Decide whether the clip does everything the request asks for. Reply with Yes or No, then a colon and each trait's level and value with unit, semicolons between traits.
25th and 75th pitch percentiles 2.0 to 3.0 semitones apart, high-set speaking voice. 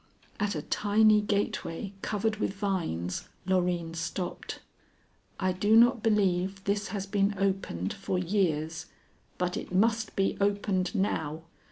Yes: narrow, 2.6 semitones; high, 195 Hz